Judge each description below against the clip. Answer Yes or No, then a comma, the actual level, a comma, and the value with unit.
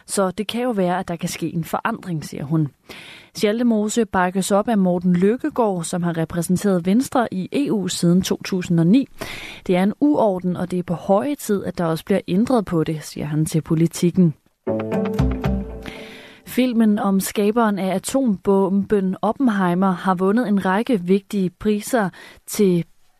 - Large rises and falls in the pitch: No, average, 3.3 semitones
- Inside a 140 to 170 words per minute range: Yes, average, 160 wpm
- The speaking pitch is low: No, high, 190 Hz